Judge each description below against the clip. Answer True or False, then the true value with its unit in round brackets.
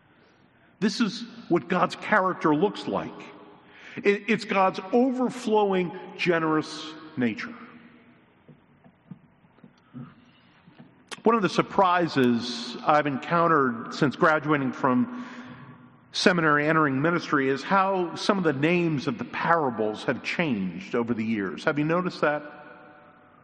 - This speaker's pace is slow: True (110 wpm)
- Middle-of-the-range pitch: True (170 Hz)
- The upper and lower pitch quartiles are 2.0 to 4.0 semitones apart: False (5.1 semitones)